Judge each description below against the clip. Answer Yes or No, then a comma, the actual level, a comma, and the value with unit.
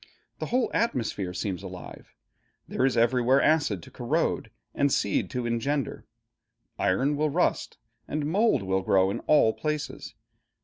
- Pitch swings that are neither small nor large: No, wide, 7.2 semitones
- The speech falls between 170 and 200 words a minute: No, average, 140 wpm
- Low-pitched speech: Yes, low, 125 Hz